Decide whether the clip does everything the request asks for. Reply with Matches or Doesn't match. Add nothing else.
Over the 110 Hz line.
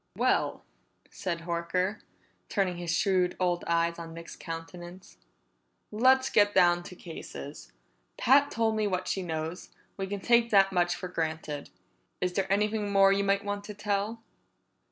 Matches